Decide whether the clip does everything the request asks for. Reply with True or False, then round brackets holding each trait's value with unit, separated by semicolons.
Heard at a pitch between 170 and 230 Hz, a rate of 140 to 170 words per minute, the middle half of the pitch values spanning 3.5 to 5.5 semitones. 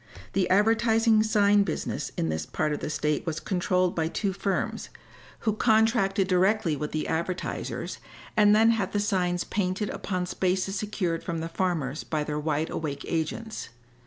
True (185 Hz; 160 wpm; 4.3 semitones)